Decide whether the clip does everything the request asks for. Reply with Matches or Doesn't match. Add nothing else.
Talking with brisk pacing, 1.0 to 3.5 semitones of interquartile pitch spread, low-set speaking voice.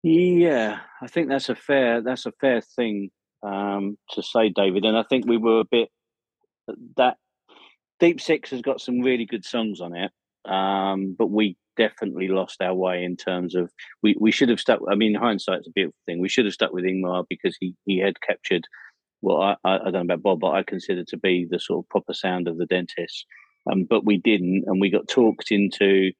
Doesn't match